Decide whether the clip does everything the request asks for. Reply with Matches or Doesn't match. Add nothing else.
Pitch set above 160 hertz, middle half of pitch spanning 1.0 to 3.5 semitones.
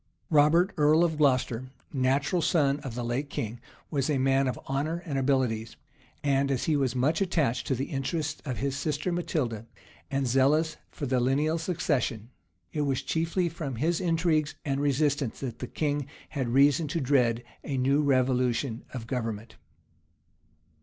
Doesn't match